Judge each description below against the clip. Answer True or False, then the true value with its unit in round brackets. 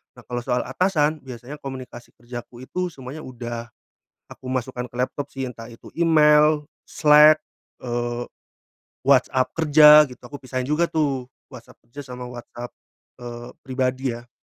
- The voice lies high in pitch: False (130 Hz)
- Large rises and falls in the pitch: False (3.5 semitones)